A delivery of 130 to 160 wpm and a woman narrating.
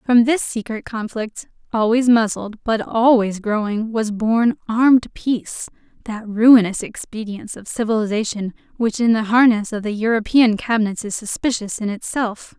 Yes: average, 145 wpm; female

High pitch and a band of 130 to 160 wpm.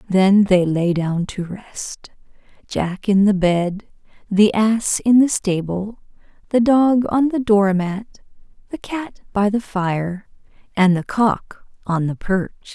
Yes: high, 200 Hz; average, 145 wpm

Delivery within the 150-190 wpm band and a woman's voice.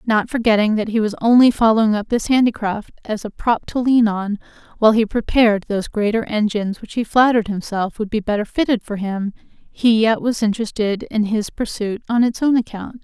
No: average, 200 wpm; female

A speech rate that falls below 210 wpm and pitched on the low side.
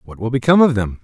No: fast, 290 wpm; low, 120 Hz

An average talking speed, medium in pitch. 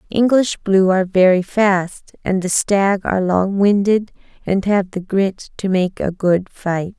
No: average, 170 wpm; high, 195 Hz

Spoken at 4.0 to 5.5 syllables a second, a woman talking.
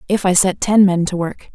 Yes: 5.2 syllables/s; female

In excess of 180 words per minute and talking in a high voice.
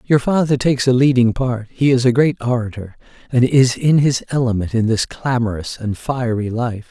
No: average, 190 wpm; low, 120 Hz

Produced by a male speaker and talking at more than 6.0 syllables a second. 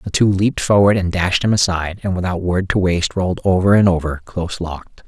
Yes: male; 6.2 syllables/s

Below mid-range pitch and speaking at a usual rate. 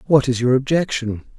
Yes: low, 130 Hz; average, 175 wpm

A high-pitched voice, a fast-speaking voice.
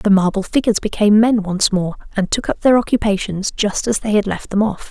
Yes: high, 205 Hz; fast, 230 wpm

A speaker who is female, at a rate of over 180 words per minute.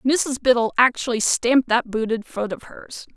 No: female; average, 170 wpm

